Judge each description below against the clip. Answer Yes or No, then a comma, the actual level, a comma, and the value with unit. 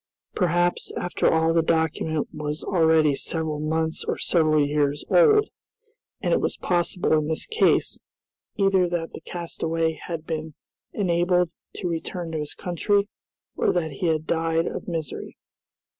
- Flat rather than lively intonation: Yes, narrow, 1.9 semitones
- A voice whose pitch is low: No, medium, 165 Hz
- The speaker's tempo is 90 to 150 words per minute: Yes, average, 145 wpm